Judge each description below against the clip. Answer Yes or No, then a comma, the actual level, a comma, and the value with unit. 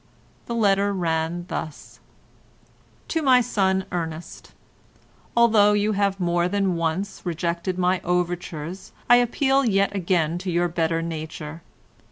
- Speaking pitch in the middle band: Yes, medium, 180 Hz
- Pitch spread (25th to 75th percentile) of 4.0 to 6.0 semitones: No, average, 3.2 semitones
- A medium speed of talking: No, slow, 120 wpm